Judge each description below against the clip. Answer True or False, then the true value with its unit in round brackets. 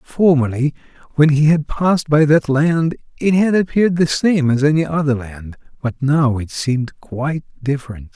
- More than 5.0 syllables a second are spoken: False (4.9 syllables/s)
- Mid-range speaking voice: True (145 Hz)